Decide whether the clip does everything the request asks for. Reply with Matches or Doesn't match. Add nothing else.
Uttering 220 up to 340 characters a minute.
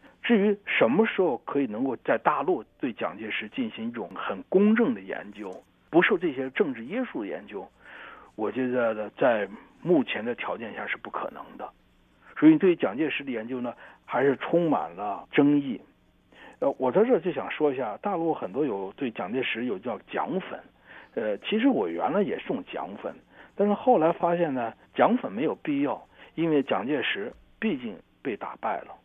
Matches